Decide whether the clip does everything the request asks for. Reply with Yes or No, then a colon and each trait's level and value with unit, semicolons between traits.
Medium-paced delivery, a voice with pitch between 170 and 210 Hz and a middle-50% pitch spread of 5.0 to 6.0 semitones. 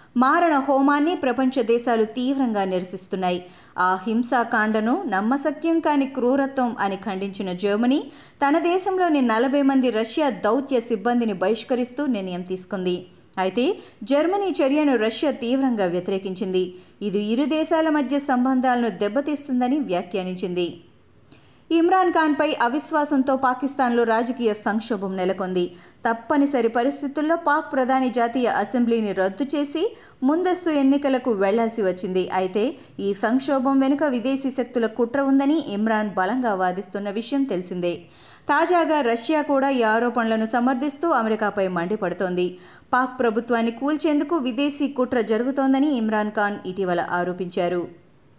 No: average, 110 wpm; high, 245 Hz; wide, 5.6 semitones